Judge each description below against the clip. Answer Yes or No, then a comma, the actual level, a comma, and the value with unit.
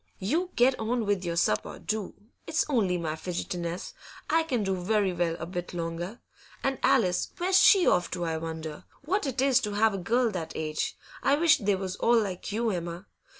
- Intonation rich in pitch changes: Yes, wide, 6.1 semitones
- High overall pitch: Yes, high, 195 Hz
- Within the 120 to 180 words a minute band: No, average, 195 wpm